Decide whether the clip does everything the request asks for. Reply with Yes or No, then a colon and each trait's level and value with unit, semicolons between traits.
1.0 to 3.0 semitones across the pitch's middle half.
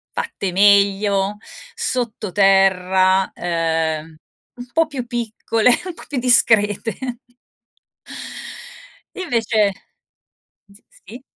No: average, 4.0 semitones